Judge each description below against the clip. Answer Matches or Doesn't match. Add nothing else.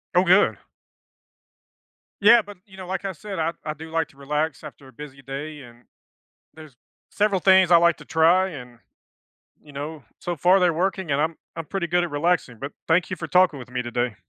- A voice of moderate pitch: Matches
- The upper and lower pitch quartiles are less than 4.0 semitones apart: Doesn't match